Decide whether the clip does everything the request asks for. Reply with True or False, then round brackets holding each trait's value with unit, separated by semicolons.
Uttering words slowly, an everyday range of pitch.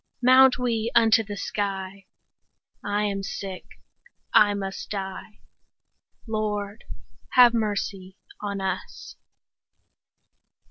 False (95 wpm; 2.3 semitones)